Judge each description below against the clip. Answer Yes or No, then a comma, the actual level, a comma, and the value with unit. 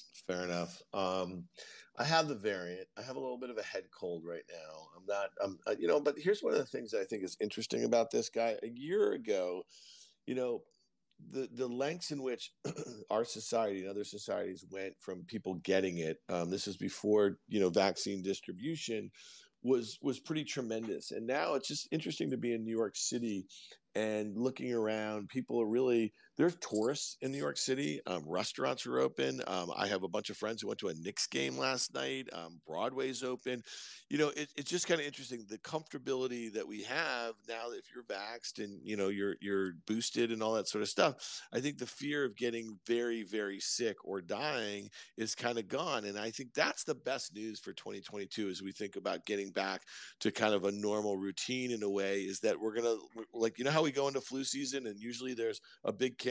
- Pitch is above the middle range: No, low, 110 Hz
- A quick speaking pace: Yes, fast, 215 wpm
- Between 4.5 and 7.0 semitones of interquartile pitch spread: Yes, average, 4.8 semitones